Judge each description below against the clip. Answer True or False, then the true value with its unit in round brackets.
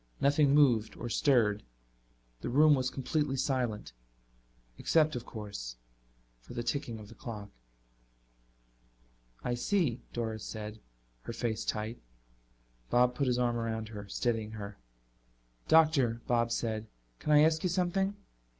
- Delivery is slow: True (130 wpm)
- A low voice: True (120 Hz)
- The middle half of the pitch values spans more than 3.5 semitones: True (4.5 semitones)